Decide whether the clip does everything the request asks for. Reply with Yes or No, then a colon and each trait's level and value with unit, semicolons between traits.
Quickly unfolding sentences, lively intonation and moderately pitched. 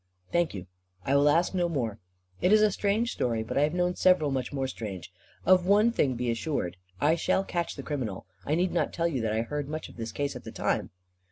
Yes: fast, 240 wpm; wide, 6.5 semitones; medium, 150 Hz